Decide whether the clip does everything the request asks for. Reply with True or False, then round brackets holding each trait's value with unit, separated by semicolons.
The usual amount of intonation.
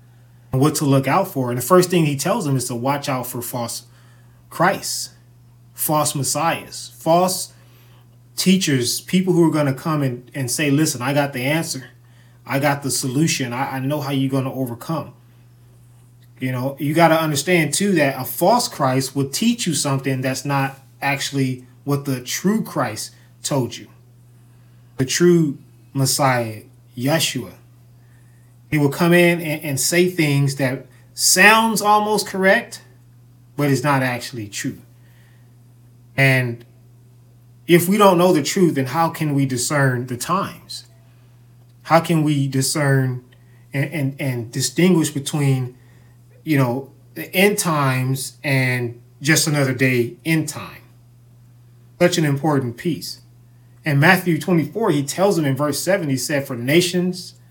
True (4.1 semitones)